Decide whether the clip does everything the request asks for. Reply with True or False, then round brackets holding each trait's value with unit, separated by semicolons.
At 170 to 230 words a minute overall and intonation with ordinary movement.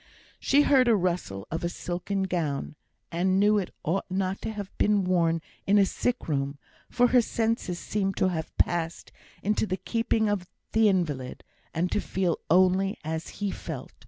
True (175 wpm; 3.3 semitones)